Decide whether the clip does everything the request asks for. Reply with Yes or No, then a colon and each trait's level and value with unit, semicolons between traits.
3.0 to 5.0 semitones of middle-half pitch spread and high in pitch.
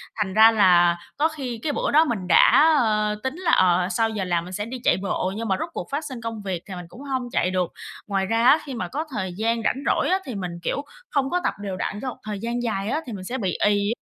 No: wide, 5.4 semitones; high, 220 Hz